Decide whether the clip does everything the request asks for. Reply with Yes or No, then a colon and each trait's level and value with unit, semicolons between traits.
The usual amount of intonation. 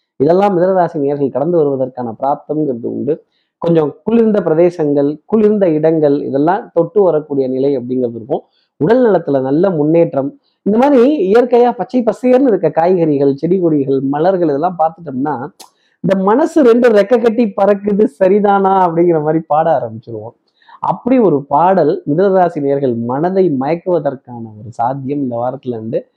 No: wide, 6.0 semitones